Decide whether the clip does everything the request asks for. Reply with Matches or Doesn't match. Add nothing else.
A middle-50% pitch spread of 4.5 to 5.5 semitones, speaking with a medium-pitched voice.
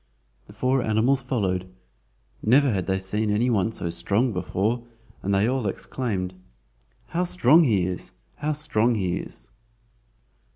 Doesn't match